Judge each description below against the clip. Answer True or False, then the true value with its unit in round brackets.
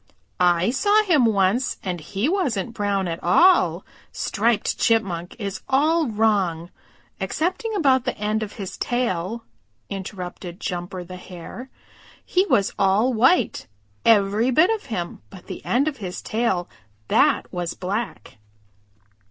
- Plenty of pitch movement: True (6.0 semitones)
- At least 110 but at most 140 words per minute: True (135 wpm)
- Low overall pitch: False (210 Hz)